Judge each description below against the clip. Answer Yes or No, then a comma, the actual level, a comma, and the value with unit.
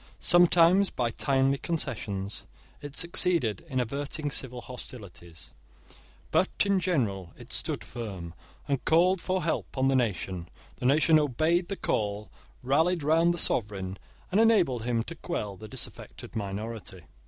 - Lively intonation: Yes, wide, 8.0 semitones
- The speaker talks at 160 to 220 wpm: No, average, 140 wpm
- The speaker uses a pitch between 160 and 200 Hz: No, low, 130 Hz